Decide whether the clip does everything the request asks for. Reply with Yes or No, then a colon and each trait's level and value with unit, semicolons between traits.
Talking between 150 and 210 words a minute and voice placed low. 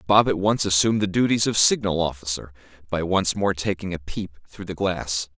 Yes: average, 200 wpm; very low, 95 Hz